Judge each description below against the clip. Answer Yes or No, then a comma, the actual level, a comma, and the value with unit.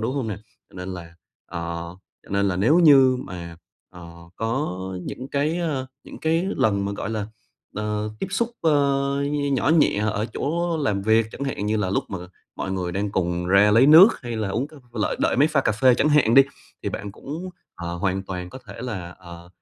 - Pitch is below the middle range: Yes, low, 110 Hz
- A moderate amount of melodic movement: No, wide, 6.8 semitones